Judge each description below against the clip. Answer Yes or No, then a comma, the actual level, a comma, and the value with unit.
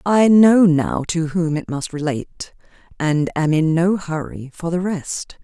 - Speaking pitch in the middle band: Yes, medium, 165 Hz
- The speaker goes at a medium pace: Yes, average, 175 wpm